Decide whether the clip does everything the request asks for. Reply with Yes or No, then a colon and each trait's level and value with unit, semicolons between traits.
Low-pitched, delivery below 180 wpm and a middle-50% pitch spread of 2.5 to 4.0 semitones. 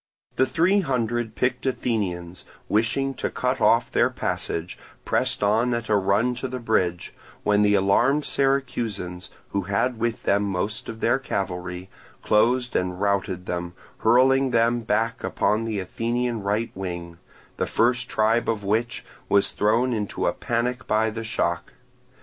Yes: low, 110 Hz; average, 150 wpm; average, 3.7 semitones